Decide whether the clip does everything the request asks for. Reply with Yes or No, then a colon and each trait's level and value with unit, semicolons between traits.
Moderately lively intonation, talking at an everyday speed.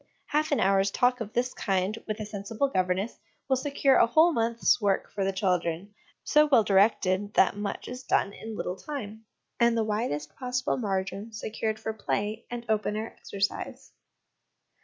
Yes: average, 3.5 semitones; average, 170 wpm